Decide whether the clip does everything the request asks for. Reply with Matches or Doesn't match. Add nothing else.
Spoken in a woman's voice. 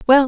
Matches